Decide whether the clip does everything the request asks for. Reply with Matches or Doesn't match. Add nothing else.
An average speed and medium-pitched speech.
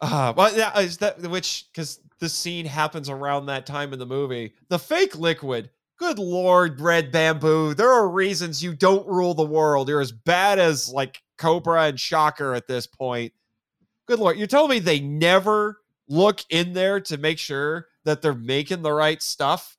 Matches